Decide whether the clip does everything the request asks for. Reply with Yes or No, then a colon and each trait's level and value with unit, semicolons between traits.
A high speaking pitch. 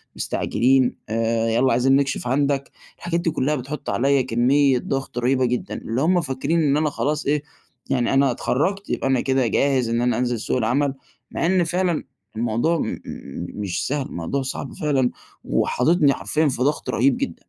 No: low, 135 Hz